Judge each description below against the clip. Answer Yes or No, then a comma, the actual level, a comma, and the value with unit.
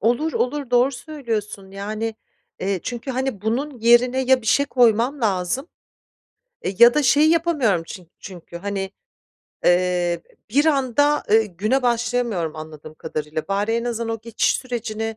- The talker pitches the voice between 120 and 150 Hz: No, high, 230 Hz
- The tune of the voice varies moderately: Yes, average, 4.7 semitones